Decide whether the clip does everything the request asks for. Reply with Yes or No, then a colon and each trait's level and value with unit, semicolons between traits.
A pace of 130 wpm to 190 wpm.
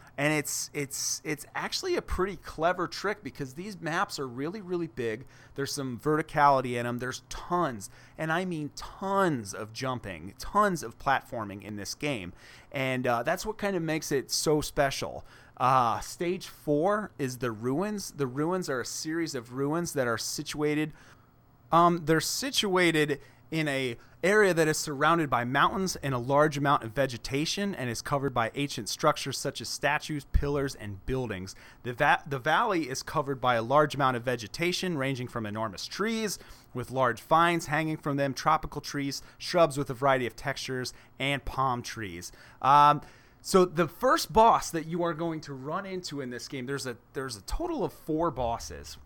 Yes: average, 180 wpm